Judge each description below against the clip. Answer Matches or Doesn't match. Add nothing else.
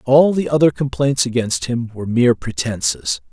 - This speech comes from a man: Matches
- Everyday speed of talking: Matches